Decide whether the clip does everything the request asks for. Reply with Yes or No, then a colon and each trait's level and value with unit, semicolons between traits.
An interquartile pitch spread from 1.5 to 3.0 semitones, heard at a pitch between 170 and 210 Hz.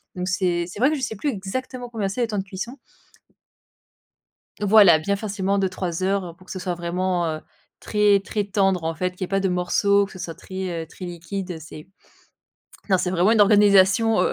Yes: narrow, 2.4 semitones; high, 190 Hz